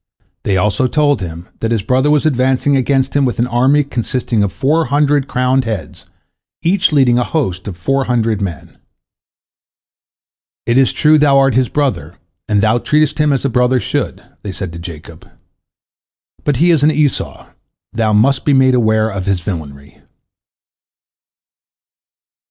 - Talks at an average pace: Yes, average, 160 wpm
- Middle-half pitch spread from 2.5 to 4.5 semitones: No, average, 5.1 semitones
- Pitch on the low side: Yes, low, 125 Hz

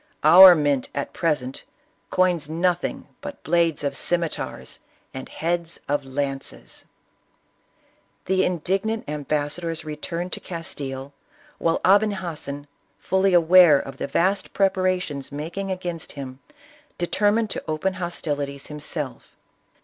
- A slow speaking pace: Yes, slow, 120 wpm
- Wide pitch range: No, average, 4.1 semitones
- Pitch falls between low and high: Yes, medium, 165 Hz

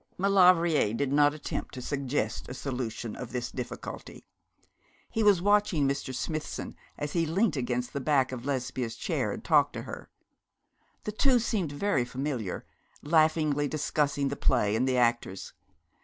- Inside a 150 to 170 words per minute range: Yes, average, 155 wpm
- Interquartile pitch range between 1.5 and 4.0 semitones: No, average, 4.5 semitones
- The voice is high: No, medium, 140 Hz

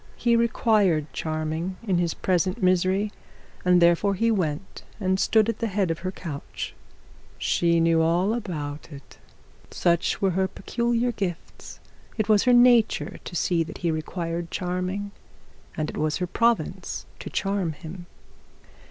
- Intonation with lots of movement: No, average, 3.7 semitones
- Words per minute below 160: Yes, average, 150 wpm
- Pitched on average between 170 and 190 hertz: Yes, medium, 185 Hz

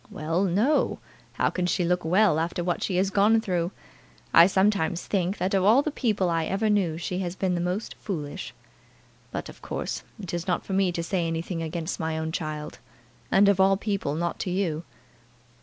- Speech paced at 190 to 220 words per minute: Yes, average, 200 wpm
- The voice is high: No, medium, 180 Hz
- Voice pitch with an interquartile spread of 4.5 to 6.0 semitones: No, average, 2.8 semitones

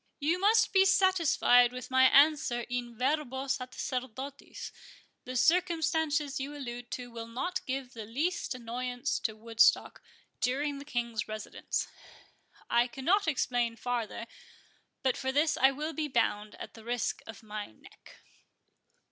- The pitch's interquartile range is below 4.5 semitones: Yes, average, 3.8 semitones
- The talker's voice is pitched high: Yes, very high, 260 Hz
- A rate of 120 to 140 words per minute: Yes, slow, 135 wpm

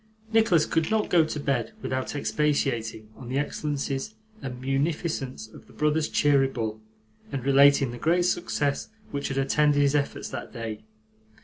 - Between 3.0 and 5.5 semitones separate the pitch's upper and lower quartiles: No, narrow, 2.6 semitones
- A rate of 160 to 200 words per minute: No, average, 150 wpm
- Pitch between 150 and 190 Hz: No, medium, 140 Hz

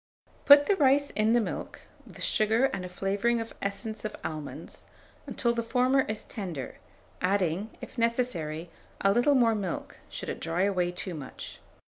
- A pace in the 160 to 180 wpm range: Yes, average, 165 wpm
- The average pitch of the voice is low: No, high, 215 Hz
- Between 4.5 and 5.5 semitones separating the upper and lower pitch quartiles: Yes, average, 4.8 semitones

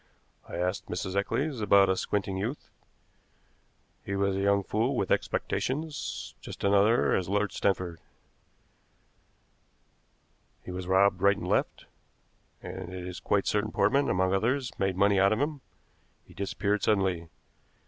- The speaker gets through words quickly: No, average, 145 wpm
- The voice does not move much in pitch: Yes, narrow, 2.3 semitones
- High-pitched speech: No, low, 100 Hz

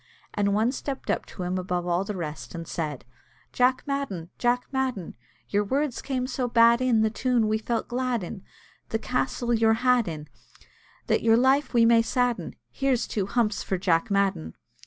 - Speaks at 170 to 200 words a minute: Yes, average, 180 wpm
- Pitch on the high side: Yes, high, 230 Hz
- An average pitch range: Yes, average, 4.7 semitones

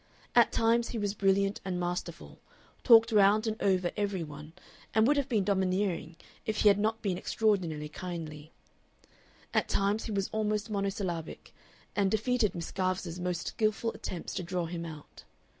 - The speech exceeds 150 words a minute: Yes, average, 160 wpm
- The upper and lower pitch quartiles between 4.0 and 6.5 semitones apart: No, average, 3.5 semitones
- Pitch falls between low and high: No, high, 195 Hz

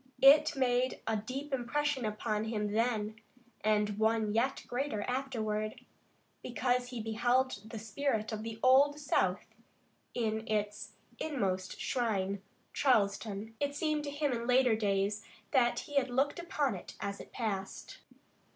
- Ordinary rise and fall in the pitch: Yes, average, 3.7 semitones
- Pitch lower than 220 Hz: No, high, 230 Hz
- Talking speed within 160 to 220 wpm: No, average, 140 wpm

